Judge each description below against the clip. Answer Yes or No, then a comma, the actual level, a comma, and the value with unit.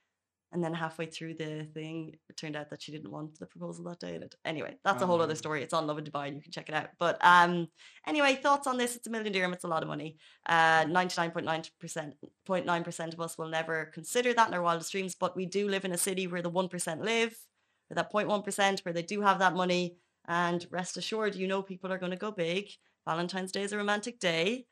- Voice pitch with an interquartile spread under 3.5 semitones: Yes, average, 3.1 semitones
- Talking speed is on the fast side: Yes, fast, 250 wpm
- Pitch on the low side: No, medium, 175 Hz